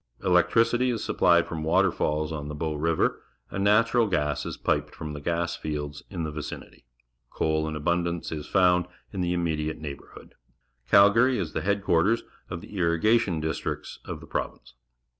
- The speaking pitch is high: No, very low, 85 Hz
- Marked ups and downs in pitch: No, average, 4.0 semitones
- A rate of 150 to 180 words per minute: Yes, average, 160 wpm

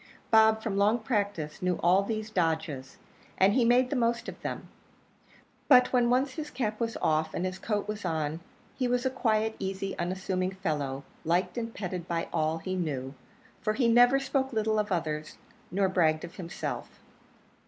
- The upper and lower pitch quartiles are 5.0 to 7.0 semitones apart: Yes, wide, 5.5 semitones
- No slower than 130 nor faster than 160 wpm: No, average, 175 wpm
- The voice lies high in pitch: Yes, high, 200 Hz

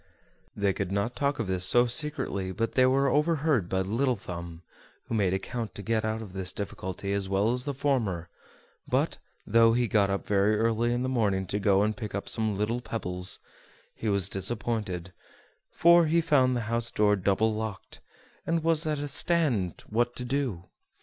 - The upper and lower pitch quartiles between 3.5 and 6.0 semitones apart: Yes, average, 4.5 semitones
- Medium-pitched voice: No, low, 110 Hz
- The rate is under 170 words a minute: No, average, 190 wpm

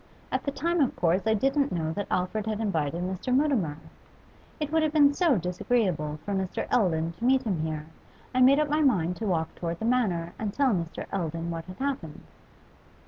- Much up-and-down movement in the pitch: Yes, wide, 7.9 semitones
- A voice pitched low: No, high, 200 Hz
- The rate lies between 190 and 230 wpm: Yes, average, 200 wpm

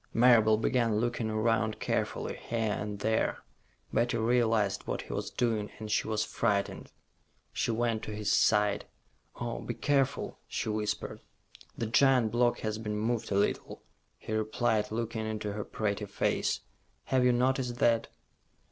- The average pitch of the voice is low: Yes, low, 110 Hz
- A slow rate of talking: No, average, 150 wpm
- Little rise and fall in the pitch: Yes, narrow, 1.9 semitones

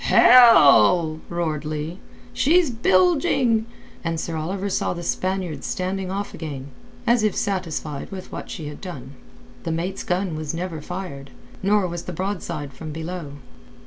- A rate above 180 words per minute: No, average, 145 wpm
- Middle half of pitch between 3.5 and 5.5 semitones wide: Yes, average, 3.8 semitones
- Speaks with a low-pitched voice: No, medium, 175 Hz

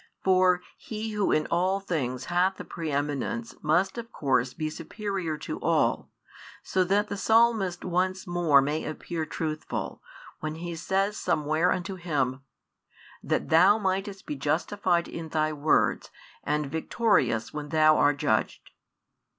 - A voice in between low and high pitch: Yes, medium, 170 Hz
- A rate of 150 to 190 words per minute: No, average, 140 wpm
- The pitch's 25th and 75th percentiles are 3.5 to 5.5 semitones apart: Yes, average, 3.9 semitones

